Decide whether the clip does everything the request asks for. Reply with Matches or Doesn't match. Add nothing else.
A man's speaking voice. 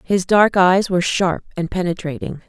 Doesn't match